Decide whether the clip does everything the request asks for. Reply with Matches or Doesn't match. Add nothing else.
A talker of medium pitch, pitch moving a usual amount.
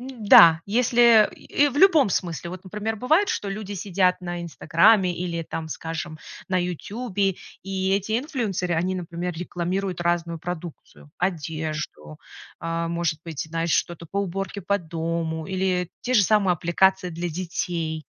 Matches